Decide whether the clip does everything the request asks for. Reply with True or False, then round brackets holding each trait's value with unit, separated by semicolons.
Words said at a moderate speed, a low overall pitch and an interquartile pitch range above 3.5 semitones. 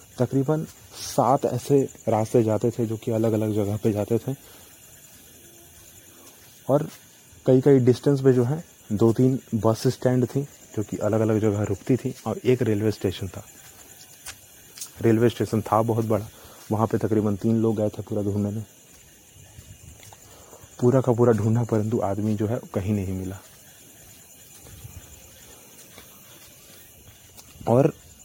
False (140 wpm; 110 Hz; 3.2 semitones)